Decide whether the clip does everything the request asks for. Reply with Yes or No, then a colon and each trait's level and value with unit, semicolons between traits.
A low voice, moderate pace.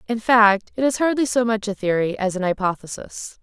No: high, 215 Hz; average, 195 wpm